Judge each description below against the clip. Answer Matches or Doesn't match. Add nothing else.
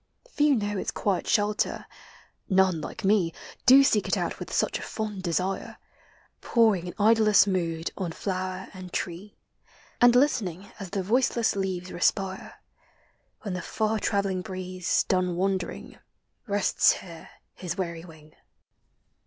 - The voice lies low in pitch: Doesn't match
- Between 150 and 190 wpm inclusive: Doesn't match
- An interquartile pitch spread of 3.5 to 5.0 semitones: Doesn't match